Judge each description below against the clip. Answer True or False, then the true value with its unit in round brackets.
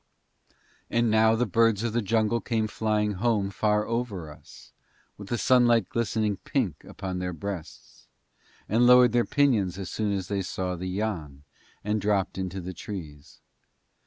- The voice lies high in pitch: False (105 Hz)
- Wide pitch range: False (3.5 semitones)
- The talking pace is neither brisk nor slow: True (160 wpm)